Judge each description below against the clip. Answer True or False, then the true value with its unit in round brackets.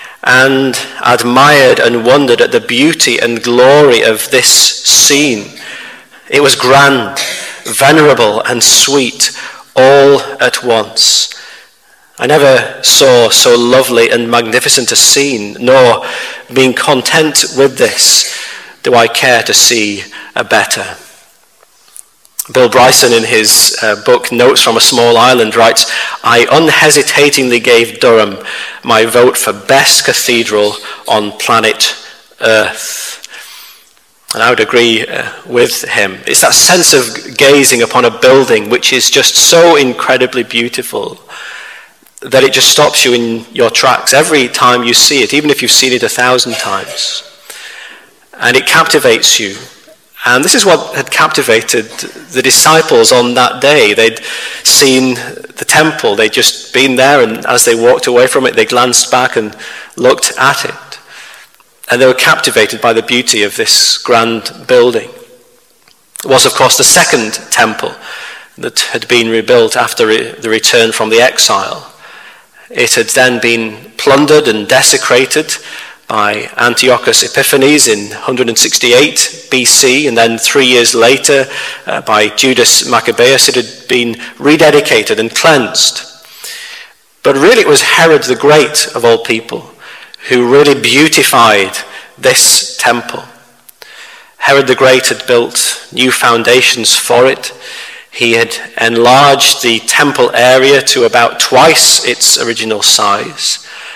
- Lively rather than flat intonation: True (6.1 semitones)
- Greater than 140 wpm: False (135 wpm)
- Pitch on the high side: False (130 Hz)